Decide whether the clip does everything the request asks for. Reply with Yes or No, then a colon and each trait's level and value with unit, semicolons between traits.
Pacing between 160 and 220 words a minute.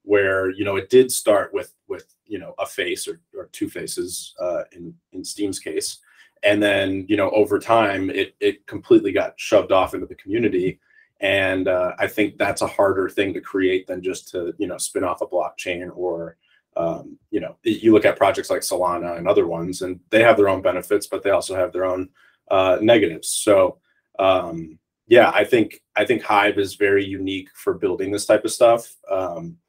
Yes: average, 200 wpm